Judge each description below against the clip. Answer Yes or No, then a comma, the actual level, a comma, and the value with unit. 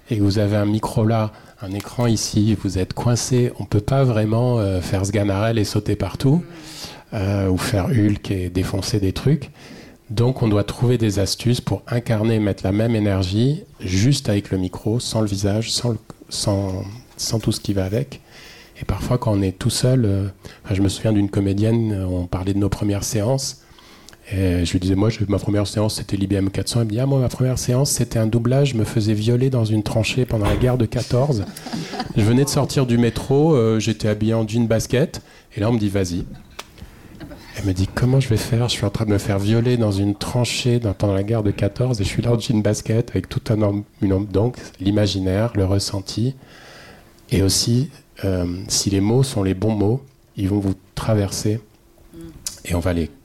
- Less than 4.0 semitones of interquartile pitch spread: Yes, average, 3.4 semitones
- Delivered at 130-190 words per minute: No, average, 210 wpm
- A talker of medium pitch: No, low, 110 Hz